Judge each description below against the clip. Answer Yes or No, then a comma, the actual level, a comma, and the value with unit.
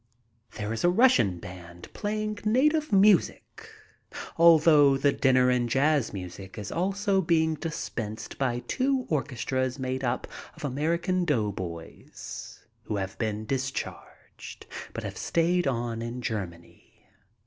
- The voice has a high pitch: No, low, 135 Hz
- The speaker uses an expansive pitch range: Yes, wide, 7.7 semitones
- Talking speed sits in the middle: No, slow, 125 wpm